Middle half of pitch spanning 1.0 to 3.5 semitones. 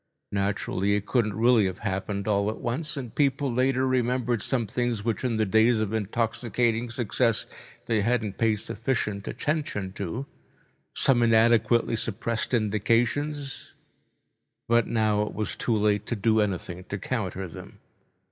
Yes: average, 2.8 semitones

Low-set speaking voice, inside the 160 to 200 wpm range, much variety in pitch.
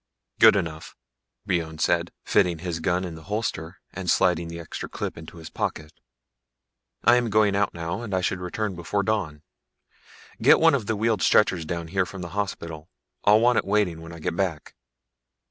No: very low, 90 Hz; average, 185 wpm; average, 3.6 semitones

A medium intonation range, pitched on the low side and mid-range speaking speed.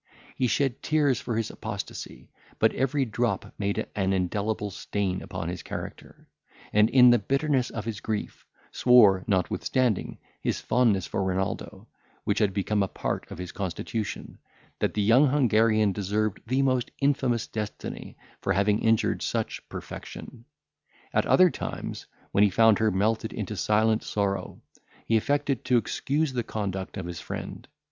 Yes: average, 3.8 semitones; low, 110 Hz; average, 155 wpm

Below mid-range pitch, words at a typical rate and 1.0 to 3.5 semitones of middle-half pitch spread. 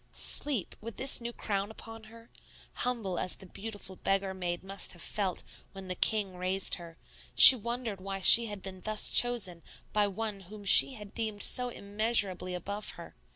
No: high, 205 Hz; average, 175 wpm; average, 3.1 semitones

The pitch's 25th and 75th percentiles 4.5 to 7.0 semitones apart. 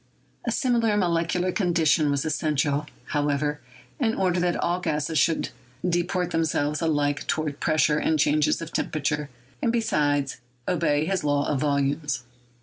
No: average, 3.1 semitones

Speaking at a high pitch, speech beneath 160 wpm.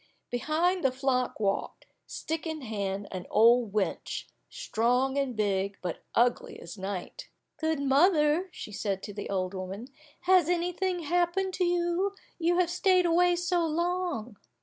Yes: very high, 290 Hz; average, 150 wpm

